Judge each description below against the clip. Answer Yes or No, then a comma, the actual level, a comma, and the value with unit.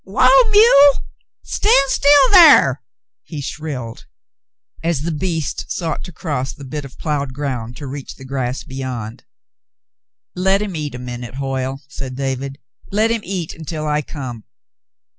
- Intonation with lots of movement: Yes, wide, 6.1 semitones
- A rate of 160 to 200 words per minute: No, average, 145 wpm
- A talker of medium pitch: Yes, medium, 145 Hz